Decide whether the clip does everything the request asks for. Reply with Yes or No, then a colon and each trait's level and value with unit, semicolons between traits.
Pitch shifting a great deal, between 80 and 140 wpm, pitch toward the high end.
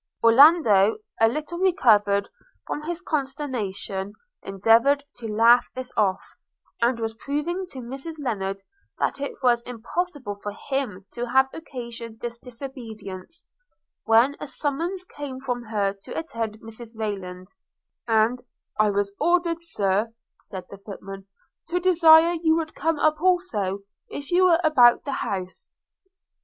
Yes: wide, 6.4 semitones; slow, 135 wpm; high, 240 Hz